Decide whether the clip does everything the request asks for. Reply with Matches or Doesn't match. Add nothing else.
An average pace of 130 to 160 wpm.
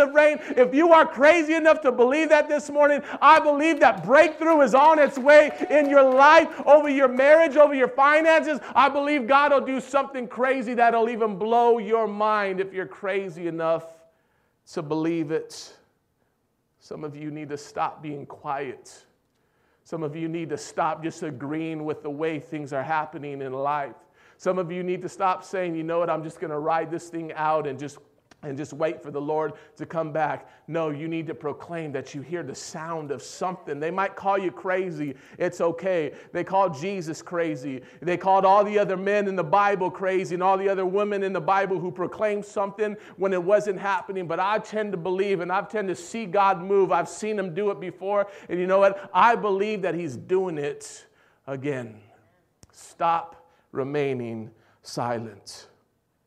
Doesn't match